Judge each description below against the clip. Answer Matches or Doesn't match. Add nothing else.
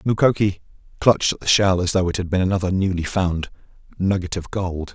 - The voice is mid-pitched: Doesn't match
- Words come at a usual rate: Matches